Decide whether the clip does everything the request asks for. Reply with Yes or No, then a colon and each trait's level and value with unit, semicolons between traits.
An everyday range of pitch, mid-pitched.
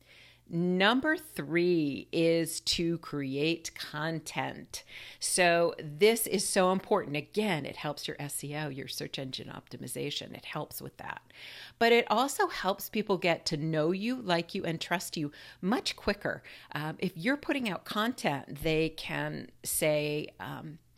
Yes: average, 4.5 semitones; medium, 165 Hz